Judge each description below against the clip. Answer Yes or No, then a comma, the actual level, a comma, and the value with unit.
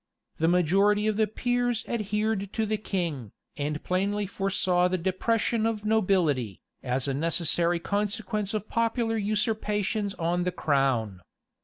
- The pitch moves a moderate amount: Yes, average, 4.2 semitones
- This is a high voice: Yes, high, 200 Hz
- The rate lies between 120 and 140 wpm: Yes, slow, 135 wpm